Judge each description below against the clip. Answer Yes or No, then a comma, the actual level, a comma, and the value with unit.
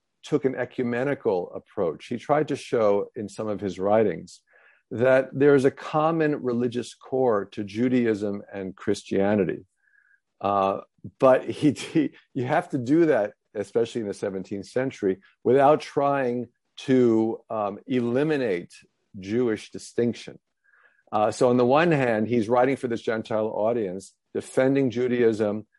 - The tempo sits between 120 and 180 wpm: Yes, slow, 135 wpm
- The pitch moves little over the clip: No, average, 3.6 semitones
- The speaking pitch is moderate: No, low, 120 Hz